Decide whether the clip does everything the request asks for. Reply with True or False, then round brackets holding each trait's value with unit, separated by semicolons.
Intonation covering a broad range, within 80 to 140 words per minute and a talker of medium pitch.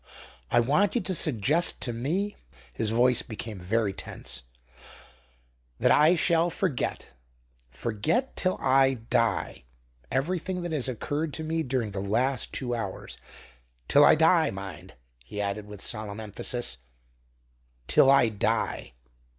False (6.8 semitones; 135 wpm; 125 Hz)